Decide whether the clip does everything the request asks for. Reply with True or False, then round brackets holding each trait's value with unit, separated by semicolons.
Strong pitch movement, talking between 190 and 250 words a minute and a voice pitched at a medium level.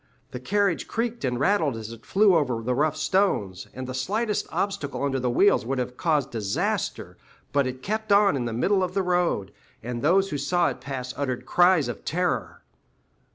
True (7.3 semitones; 195 wpm; 145 Hz)